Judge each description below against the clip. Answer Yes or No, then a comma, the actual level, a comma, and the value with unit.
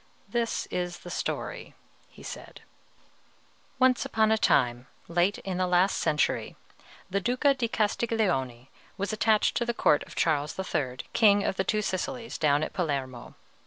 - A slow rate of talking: No, average, 155 wpm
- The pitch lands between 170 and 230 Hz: Yes, high, 190 Hz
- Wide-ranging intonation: Yes, wide, 6.7 semitones